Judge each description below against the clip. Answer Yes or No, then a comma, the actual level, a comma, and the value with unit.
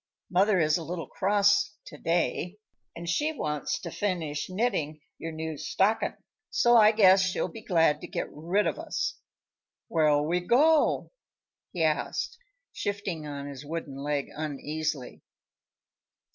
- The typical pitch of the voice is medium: Yes, medium, 170 Hz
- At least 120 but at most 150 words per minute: Yes, average, 140 wpm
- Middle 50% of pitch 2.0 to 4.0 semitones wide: No, average, 5.1 semitones